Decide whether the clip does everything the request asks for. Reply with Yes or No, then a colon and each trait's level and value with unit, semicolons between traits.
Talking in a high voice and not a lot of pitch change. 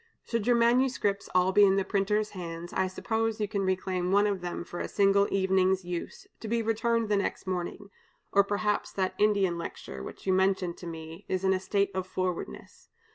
Yes: high, 195 Hz; narrow, 2.2 semitones